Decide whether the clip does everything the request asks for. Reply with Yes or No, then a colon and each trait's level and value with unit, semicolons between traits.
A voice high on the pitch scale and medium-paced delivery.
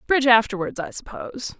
Yes: high, 240 Hz; average, 150 wpm